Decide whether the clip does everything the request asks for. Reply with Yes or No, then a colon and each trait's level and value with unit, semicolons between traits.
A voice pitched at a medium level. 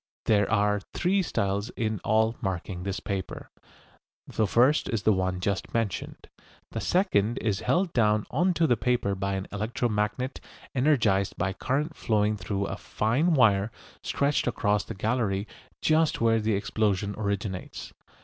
No: low, 110 Hz